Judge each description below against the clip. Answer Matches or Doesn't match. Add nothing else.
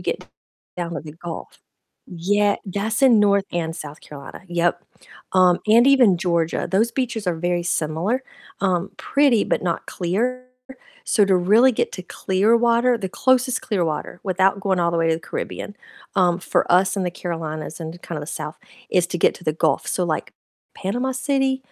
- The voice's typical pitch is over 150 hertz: Matches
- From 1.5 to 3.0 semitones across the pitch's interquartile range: Doesn't match